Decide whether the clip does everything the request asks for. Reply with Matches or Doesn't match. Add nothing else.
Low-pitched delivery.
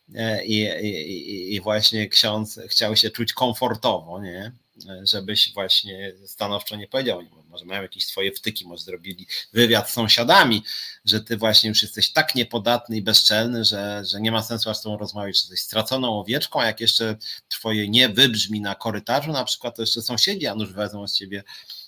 Matches